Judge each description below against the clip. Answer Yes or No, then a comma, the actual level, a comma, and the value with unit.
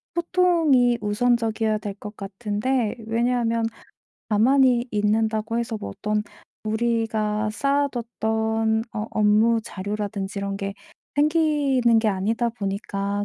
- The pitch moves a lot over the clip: No, narrow, 2.5 semitones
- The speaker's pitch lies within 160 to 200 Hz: No, high, 220 Hz